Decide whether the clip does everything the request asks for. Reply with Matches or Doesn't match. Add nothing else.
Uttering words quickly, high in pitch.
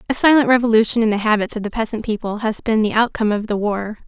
Matches